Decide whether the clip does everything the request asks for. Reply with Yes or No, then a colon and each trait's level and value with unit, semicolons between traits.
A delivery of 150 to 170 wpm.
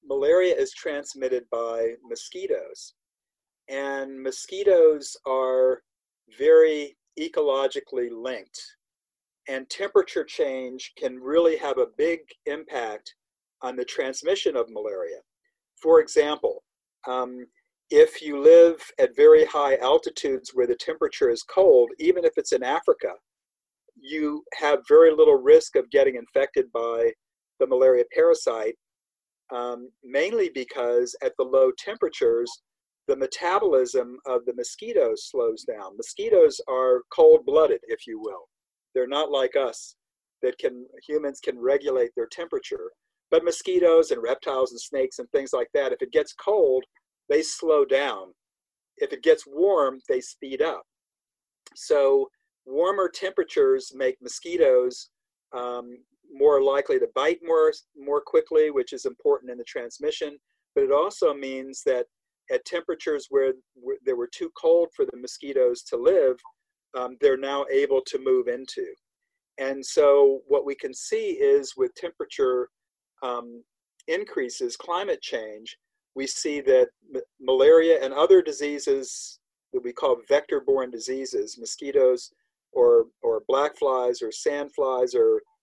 No: slow, 135 wpm